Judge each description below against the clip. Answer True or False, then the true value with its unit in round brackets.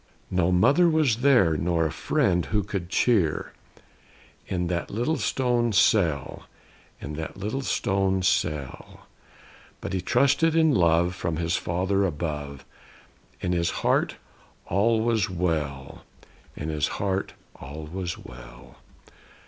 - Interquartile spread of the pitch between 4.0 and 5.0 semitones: True (4.7 semitones)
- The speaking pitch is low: True (90 Hz)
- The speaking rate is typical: False (125 wpm)